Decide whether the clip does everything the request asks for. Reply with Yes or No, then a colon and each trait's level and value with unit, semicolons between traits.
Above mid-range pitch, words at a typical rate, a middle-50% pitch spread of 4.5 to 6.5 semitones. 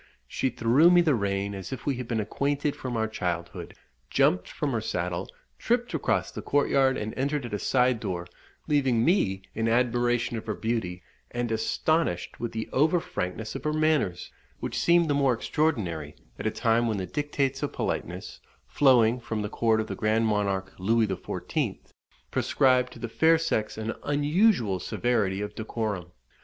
No: low, 115 Hz; average, 175 wpm; average, 5.1 semitones